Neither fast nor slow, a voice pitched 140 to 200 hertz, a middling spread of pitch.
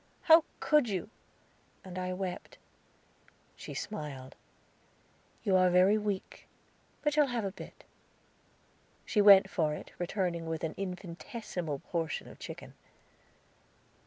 No: slow, 120 wpm; medium, 185 Hz; average, 3.7 semitones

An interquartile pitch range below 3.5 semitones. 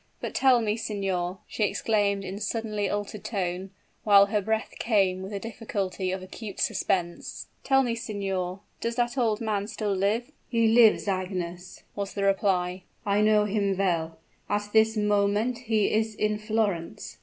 Yes: narrow, 2.4 semitones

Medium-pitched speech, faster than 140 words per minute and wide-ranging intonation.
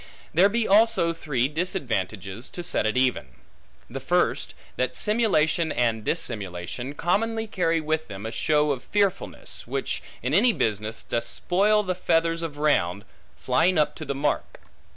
Yes: medium, 155 Hz; average, 150 wpm; wide, 7.5 semitones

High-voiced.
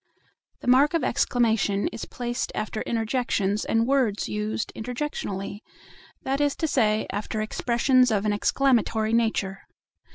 Yes: high, 225 Hz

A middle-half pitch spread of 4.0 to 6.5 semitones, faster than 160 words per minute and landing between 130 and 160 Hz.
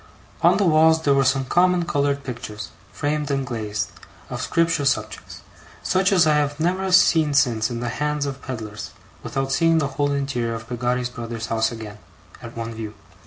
Yes: average, 4.8 semitones; average, 180 wpm; low, 135 Hz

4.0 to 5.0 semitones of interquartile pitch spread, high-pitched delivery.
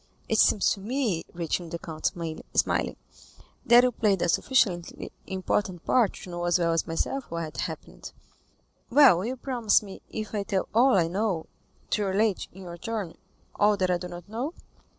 Yes: average, 4.5 semitones; high, 195 Hz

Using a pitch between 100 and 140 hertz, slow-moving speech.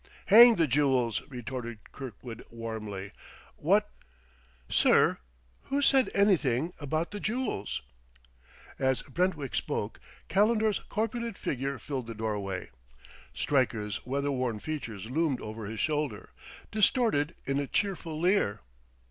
Yes: low, 135 Hz; slow, 115 wpm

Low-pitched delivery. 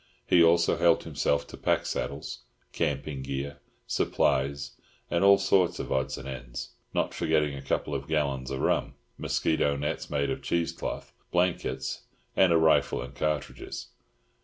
Yes: very low, 70 Hz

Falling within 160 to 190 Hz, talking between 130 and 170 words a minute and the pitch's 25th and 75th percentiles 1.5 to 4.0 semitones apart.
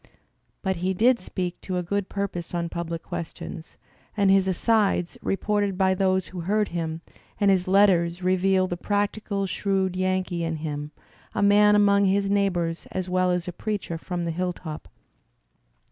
Yes: medium, 185 Hz; average, 160 wpm; narrow, 2.4 semitones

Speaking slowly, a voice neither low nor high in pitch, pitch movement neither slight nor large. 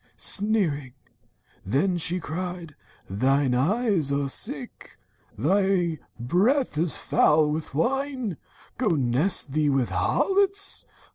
No: slow, 110 wpm; medium, 165 Hz; wide, 6.4 semitones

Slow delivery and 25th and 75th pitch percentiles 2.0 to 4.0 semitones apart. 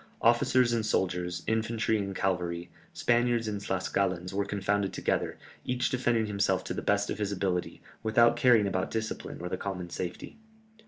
No: average, 160 wpm; average, 3.6 semitones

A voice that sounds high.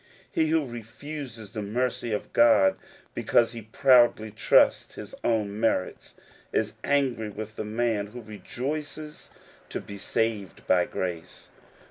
No: low, 115 Hz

